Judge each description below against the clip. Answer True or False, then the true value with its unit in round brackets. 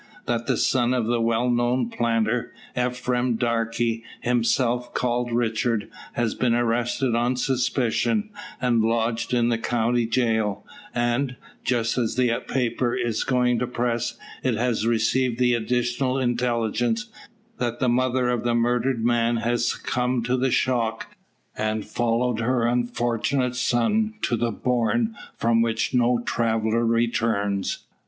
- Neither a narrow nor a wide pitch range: False (1.3 semitones)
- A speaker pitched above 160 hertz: False (120 Hz)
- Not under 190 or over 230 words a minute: False (135 wpm)